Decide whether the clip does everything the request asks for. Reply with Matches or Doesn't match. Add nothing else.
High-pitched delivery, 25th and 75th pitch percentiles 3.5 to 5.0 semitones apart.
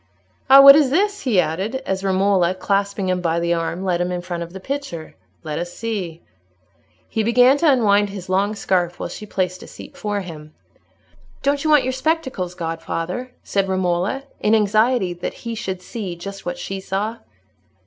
Matches